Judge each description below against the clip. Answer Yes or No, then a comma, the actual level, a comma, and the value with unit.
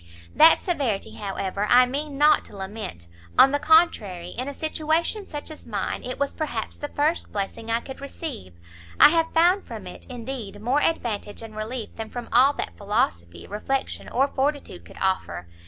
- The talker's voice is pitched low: No, very high, 250 Hz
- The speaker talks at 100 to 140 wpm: No, average, 175 wpm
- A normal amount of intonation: No, wide, 6.1 semitones